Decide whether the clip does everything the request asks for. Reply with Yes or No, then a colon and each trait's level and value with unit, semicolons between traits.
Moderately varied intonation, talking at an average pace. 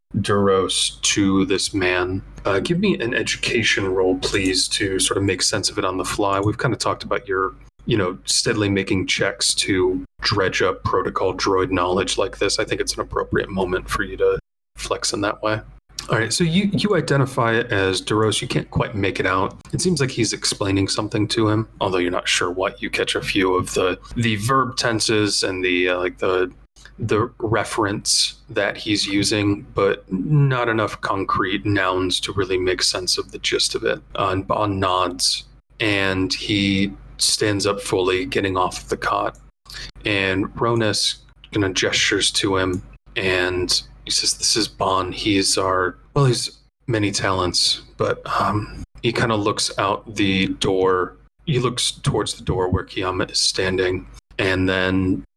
Yes: average, 4.3 semitones; average, 180 wpm